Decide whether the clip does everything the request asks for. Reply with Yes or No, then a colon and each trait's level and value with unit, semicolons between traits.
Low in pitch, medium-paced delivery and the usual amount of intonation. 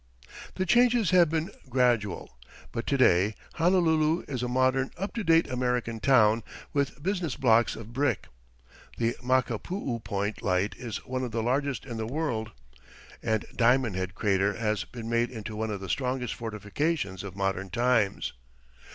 Yes: low, 120 Hz; average, 160 wpm; average, 4.7 semitones